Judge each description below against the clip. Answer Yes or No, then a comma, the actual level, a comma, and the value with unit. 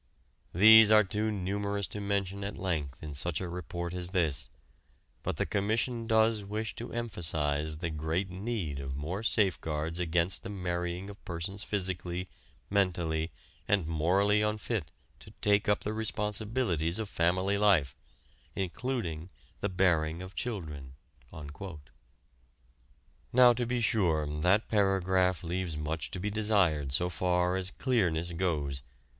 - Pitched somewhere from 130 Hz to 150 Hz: No, very low, 90 Hz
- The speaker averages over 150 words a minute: No, slow, 135 wpm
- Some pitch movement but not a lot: Yes, average, 4.2 semitones